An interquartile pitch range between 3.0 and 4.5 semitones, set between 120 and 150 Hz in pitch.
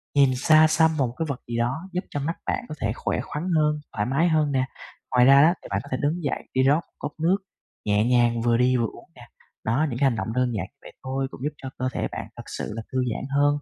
Yes: average, 3.8 semitones; low, 135 Hz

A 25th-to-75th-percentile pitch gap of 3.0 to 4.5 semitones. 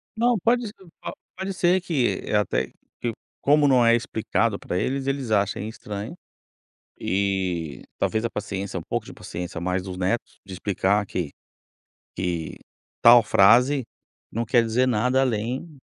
No: wide, 5.4 semitones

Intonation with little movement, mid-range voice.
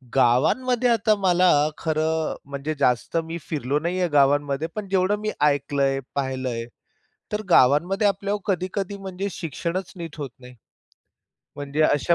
No: wide, 5.4 semitones; medium, 160 Hz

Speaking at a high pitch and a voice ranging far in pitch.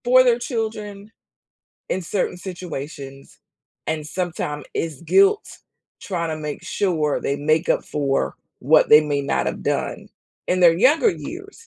No: medium, 170 Hz; wide, 6.7 semitones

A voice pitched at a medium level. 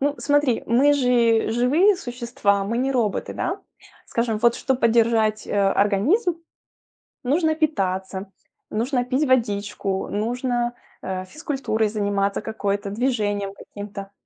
No: high, 230 Hz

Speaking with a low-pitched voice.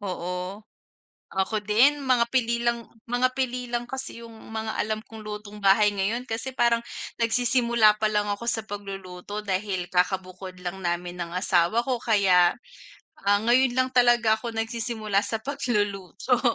No: high, 220 Hz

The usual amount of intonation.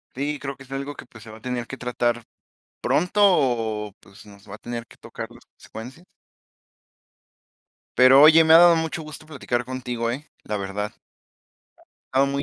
Yes: average, 4.2 semitones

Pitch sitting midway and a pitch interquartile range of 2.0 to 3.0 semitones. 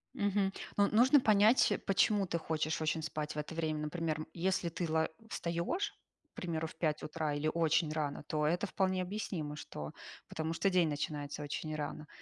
No: medium, 160 Hz; average, 3.5 semitones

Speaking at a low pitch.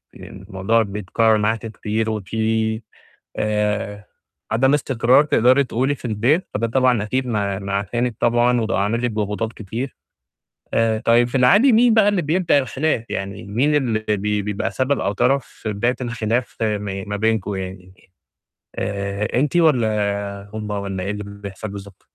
Yes: low, 110 Hz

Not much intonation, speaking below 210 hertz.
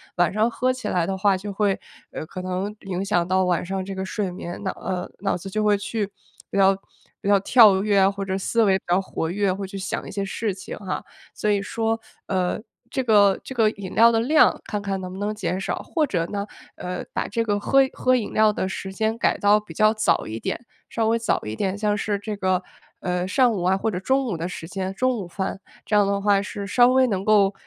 Yes: narrow, 2.3 semitones; high, 200 Hz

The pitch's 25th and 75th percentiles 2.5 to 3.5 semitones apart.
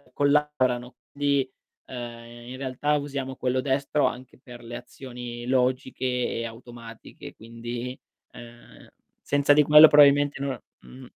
Yes: average, 2.9 semitones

